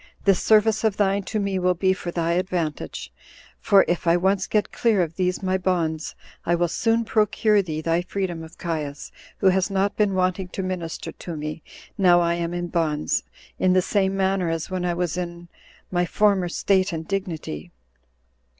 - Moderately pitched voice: Yes, medium, 180 Hz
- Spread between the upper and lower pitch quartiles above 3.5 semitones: No, narrow, 2.4 semitones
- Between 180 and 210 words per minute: Yes, average, 185 wpm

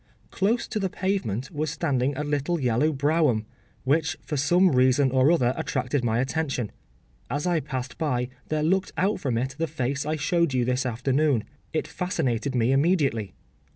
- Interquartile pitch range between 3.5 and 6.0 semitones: Yes, average, 4.2 semitones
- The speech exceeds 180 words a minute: No, average, 170 wpm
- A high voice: No, medium, 140 Hz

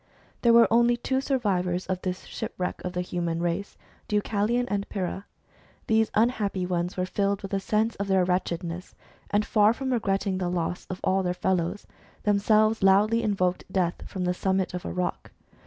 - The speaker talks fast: No, average, 175 wpm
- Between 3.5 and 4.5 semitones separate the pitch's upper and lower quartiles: No, average, 3.0 semitones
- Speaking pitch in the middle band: No, high, 195 Hz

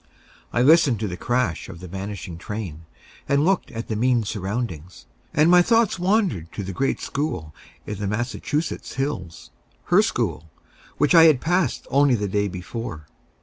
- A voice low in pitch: Yes, low, 115 Hz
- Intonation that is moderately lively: No, wide, 7.8 semitones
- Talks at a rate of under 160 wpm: No, average, 165 wpm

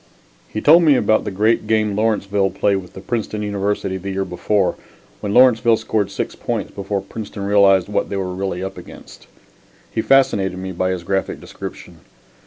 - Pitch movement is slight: Yes, narrow, 2.2 semitones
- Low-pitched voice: Yes, low, 100 Hz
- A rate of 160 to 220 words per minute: Yes, average, 180 wpm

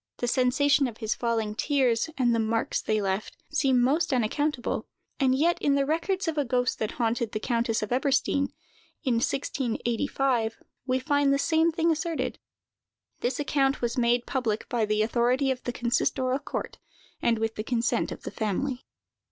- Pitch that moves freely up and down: No, average, 3.3 semitones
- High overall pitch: Yes, very high, 250 Hz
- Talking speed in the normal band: Yes, average, 170 wpm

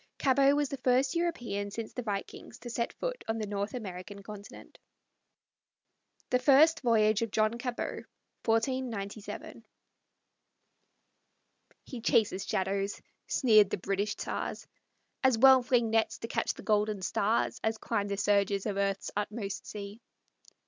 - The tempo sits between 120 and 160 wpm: Yes, slow, 135 wpm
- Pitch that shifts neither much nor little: Yes, average, 3.6 semitones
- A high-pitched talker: Yes, high, 220 Hz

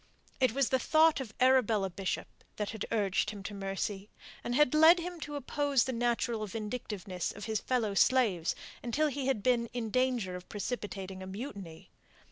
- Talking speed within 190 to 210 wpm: No, average, 175 wpm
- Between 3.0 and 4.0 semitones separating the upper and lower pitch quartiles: No, average, 4.6 semitones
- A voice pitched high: Yes, high, 230 Hz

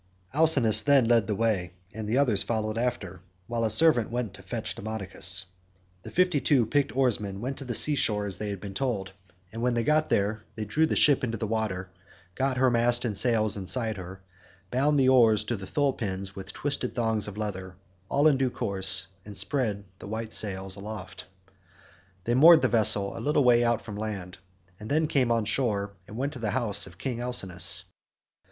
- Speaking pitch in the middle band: No, low, 110 Hz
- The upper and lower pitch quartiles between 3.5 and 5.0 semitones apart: Yes, average, 4.1 semitones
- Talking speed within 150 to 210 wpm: Yes, average, 200 wpm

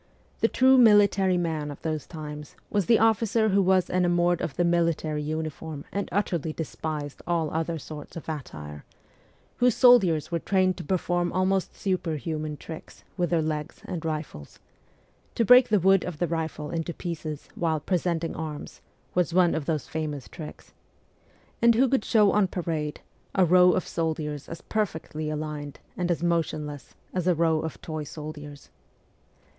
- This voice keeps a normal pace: Yes, average, 165 wpm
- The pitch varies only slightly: No, average, 3.2 semitones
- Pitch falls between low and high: Yes, medium, 165 Hz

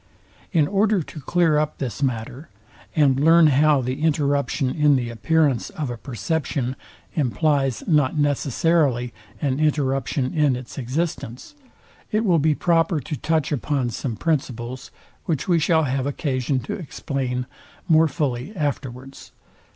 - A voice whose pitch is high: No, medium, 145 Hz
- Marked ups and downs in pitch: No, average, 3.5 semitones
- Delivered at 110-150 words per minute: Yes, slow, 135 wpm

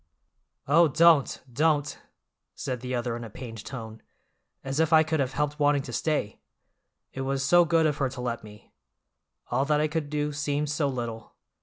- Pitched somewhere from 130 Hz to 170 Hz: Yes, medium, 140 Hz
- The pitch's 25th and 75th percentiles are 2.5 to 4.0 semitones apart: Yes, average, 3.4 semitones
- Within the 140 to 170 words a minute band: No, average, 185 wpm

